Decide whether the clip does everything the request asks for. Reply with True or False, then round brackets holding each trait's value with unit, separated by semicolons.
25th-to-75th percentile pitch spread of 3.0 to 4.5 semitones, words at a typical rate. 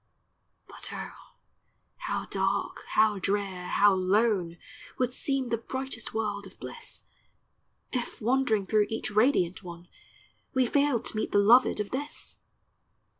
False (3.9 semitones; 130 wpm)